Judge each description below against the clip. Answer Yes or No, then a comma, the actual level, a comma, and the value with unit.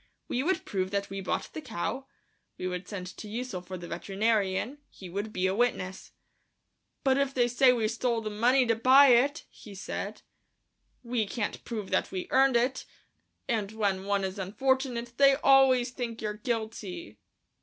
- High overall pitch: Yes, high, 225 Hz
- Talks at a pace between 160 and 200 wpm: Yes, average, 175 wpm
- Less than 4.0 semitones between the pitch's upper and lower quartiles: No, average, 4.5 semitones